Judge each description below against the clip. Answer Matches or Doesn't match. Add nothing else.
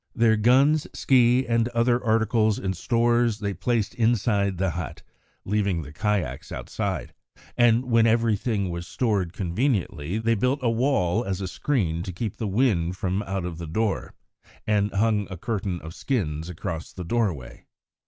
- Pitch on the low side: Matches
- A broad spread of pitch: Doesn't match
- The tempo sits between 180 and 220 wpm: Doesn't match